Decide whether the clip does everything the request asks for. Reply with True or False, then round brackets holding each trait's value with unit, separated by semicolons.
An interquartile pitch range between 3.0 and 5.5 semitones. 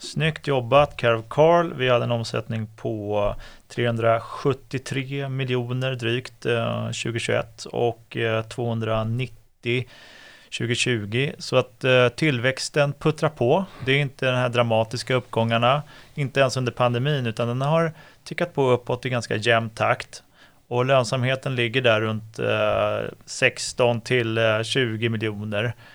False (2.6 semitones)